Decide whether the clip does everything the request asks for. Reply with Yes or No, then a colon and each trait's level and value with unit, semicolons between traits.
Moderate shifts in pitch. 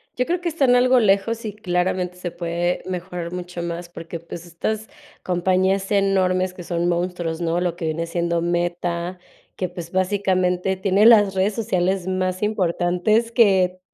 No: narrow, 2.1 semitones